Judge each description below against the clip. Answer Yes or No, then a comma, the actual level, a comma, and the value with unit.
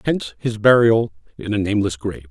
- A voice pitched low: Yes, low, 105 Hz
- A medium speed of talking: Yes, average, 180 wpm